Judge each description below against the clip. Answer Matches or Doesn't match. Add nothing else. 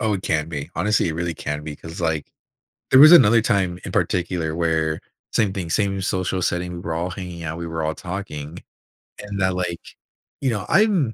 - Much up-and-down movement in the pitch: Doesn't match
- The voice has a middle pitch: Doesn't match